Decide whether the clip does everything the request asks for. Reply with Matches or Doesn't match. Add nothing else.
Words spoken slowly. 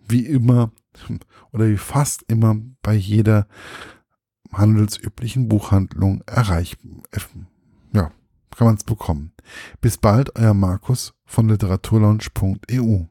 Matches